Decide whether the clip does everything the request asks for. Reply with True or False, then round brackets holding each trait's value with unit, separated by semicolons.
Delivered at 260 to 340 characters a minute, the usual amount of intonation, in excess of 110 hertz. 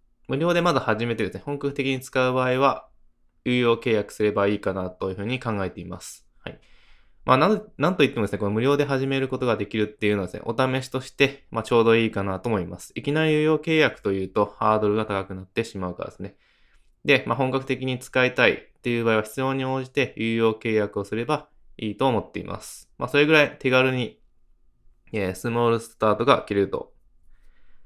False (425 characters per minute; 4.2 semitones; 120 Hz)